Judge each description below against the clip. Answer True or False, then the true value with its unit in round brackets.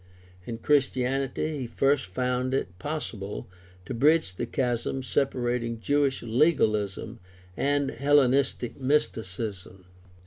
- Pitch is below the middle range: True (130 Hz)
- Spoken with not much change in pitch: False (3.7 semitones)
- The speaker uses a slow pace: True (105 wpm)